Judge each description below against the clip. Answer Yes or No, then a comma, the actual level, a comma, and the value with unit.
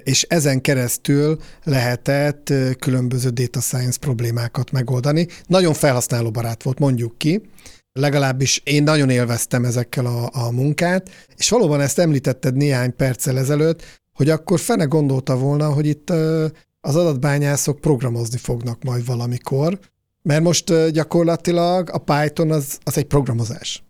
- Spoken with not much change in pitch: No, average, 3.9 semitones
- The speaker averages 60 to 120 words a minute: No, average, 130 wpm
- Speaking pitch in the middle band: Yes, medium, 145 Hz